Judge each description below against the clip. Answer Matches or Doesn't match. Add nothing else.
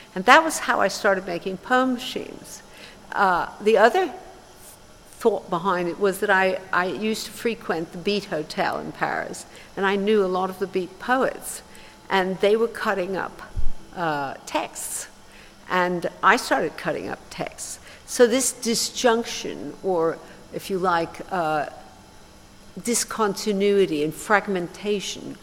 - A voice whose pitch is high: Matches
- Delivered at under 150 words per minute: Matches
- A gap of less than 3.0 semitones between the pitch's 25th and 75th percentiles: Doesn't match